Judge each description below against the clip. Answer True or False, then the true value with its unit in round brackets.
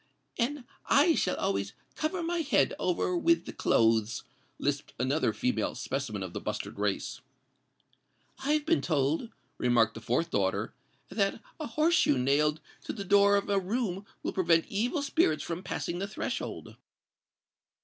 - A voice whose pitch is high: True (195 Hz)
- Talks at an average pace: True (150 wpm)